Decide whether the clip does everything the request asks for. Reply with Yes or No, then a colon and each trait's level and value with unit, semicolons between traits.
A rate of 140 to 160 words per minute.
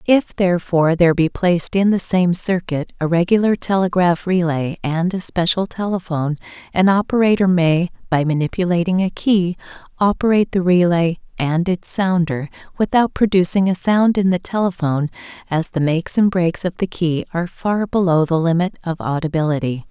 Yes: average, 155 wpm